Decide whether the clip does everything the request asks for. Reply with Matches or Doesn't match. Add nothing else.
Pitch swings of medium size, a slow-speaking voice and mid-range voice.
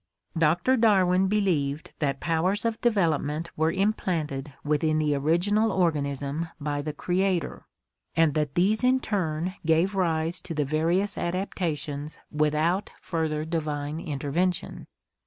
Matches